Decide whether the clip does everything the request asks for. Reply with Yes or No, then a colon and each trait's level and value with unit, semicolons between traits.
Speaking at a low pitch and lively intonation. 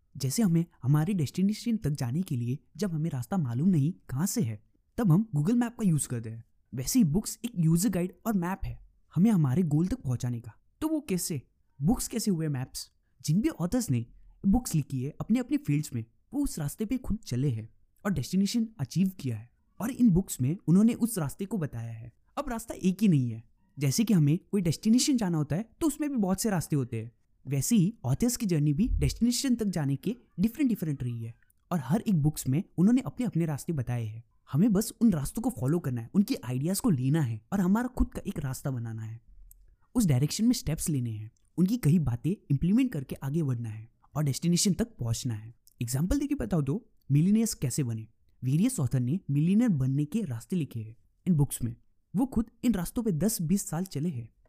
No: medium, 160 Hz; wide, 8.5 semitones